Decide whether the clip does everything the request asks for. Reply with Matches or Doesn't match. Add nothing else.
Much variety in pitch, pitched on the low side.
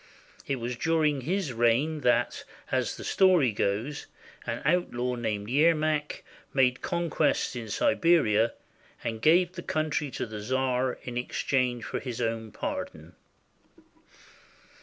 Doesn't match